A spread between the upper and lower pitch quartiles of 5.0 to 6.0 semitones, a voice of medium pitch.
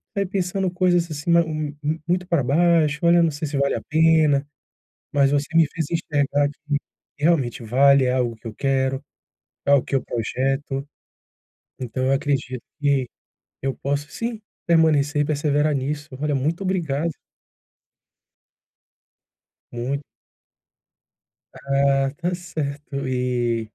No: average, 3.2 semitones; medium, 145 Hz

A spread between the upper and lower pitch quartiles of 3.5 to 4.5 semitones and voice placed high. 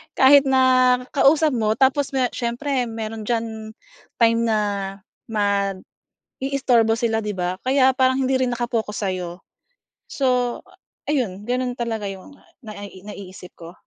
Yes: average, 3.8 semitones; high, 235 Hz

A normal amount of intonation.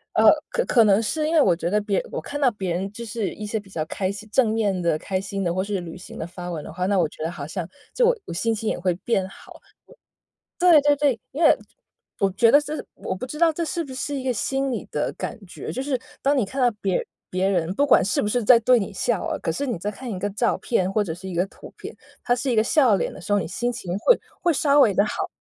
No: wide, 5.9 semitones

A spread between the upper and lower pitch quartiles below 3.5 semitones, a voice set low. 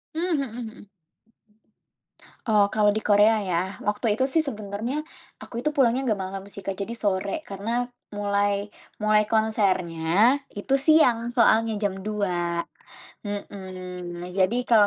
No: average, 3.0 semitones; high, 210 Hz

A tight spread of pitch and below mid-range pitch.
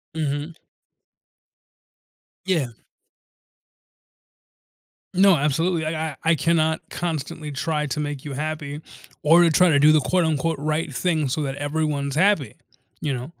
No: narrow, 2.3 semitones; medium, 155 Hz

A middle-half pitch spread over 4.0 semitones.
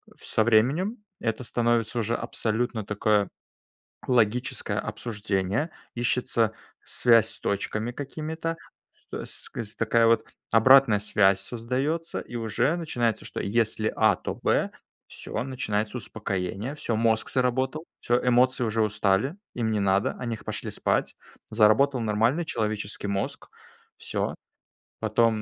No: average, 2.9 semitones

